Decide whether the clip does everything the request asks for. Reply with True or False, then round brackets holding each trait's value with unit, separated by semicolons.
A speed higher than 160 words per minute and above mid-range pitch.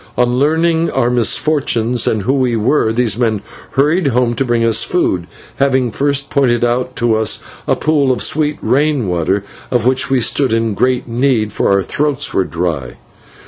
False (180 wpm; 125 Hz)